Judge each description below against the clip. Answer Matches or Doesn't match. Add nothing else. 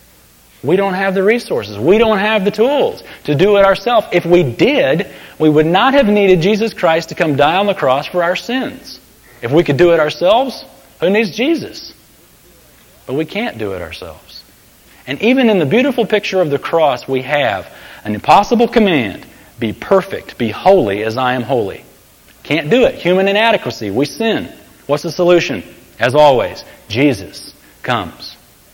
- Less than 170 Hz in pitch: Doesn't match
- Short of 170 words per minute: Doesn't match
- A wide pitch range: Matches